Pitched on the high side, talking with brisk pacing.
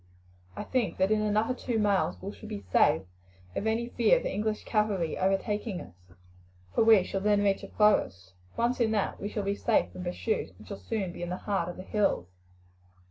Yes: high, 205 Hz; fast, 210 wpm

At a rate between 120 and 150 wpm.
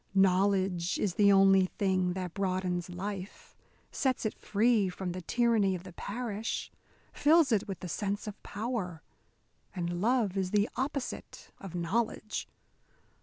Yes: average, 140 wpm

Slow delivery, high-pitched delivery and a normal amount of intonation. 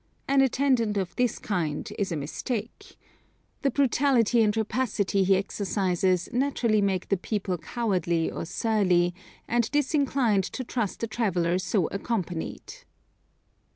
Yes: slow, 125 wpm; high, 210 Hz; average, 4.6 semitones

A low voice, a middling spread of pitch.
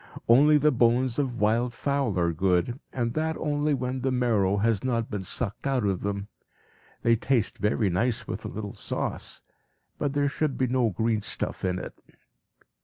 Yes: low, 120 Hz; average, 4.3 semitones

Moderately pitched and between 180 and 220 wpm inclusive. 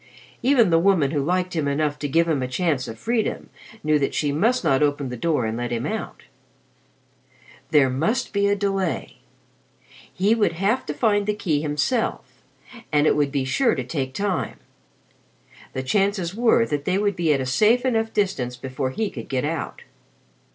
Yes: medium, 165 Hz; average, 185 wpm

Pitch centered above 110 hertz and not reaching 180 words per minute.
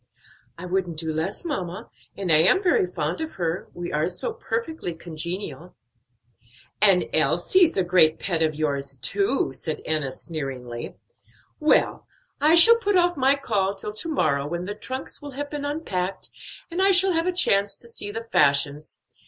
Yes: medium, 185 Hz; average, 170 wpm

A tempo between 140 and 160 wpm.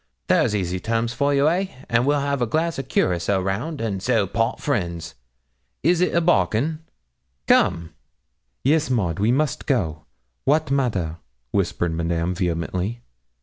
Yes: average, 150 wpm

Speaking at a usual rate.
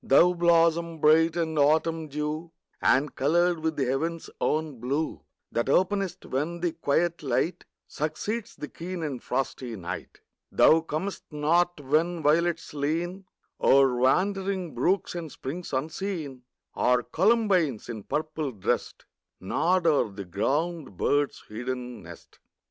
No: slow, 130 wpm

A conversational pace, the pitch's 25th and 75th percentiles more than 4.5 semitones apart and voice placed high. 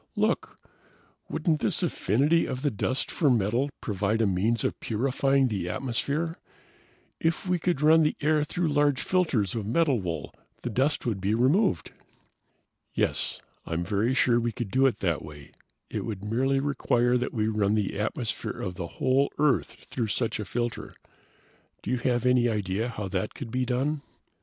No: average, 170 wpm; average, 4.9 semitones; low, 120 Hz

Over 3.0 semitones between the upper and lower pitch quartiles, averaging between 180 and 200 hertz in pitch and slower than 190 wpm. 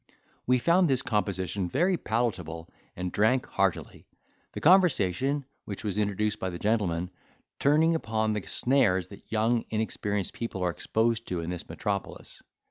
No: average, 5.2 semitones; low, 110 Hz; average, 145 wpm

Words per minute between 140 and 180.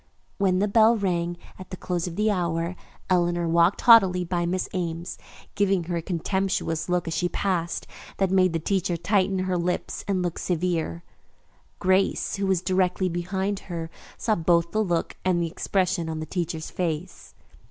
Yes: average, 175 wpm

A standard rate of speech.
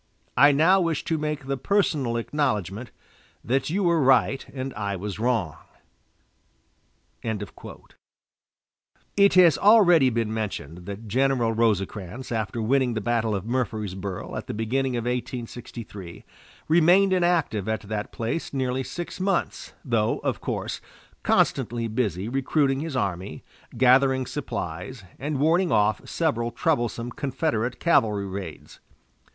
No: slow, 125 wpm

